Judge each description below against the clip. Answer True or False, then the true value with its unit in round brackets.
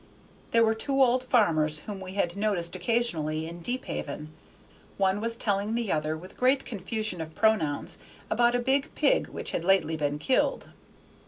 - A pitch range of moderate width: False (6.4 semitones)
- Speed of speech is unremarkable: True (165 wpm)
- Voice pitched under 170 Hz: False (200 Hz)